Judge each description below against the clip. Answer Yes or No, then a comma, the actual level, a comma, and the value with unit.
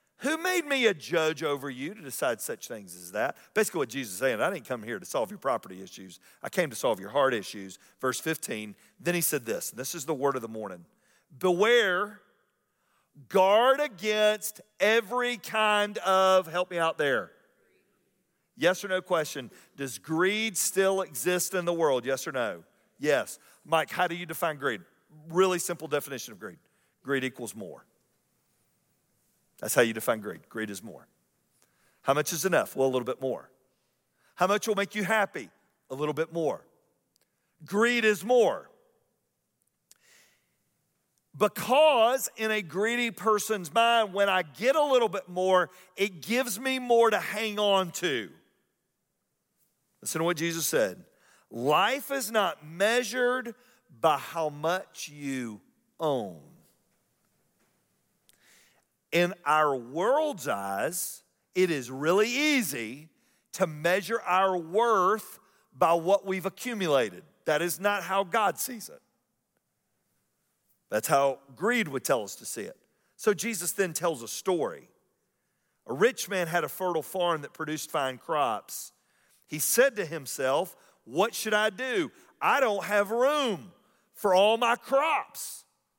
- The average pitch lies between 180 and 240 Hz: Yes, medium, 185 Hz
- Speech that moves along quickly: No, average, 150 wpm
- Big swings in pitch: Yes, wide, 5.9 semitones